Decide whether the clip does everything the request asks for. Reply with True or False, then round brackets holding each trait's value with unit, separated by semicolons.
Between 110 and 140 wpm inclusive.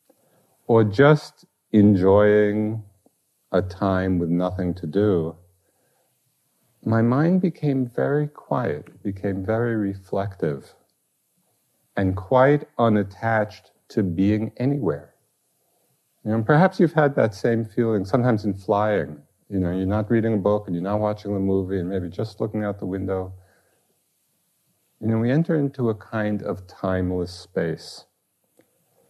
True (135 wpm)